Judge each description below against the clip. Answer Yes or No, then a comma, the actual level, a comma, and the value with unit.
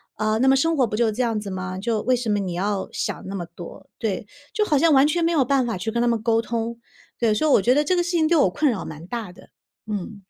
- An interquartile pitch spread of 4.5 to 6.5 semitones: Yes, average, 5.1 semitones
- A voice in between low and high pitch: No, high, 230 Hz